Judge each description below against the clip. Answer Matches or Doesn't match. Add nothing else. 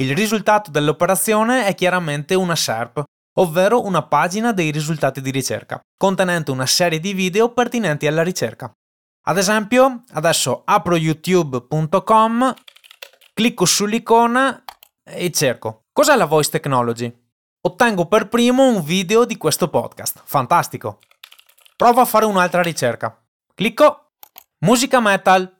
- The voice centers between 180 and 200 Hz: Matches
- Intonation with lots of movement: Matches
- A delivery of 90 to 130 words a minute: Matches